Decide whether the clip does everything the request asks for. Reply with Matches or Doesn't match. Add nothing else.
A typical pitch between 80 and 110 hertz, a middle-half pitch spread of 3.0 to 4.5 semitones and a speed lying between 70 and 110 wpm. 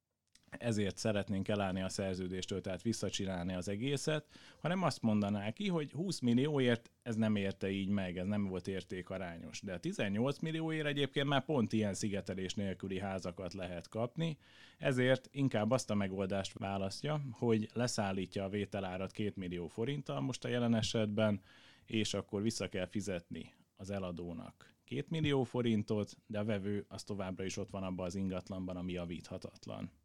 Doesn't match